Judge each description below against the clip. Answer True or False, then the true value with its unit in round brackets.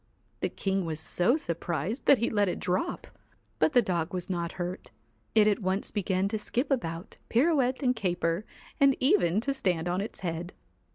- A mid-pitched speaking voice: False (195 Hz)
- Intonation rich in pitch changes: True (5.7 semitones)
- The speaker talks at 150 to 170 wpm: False (180 wpm)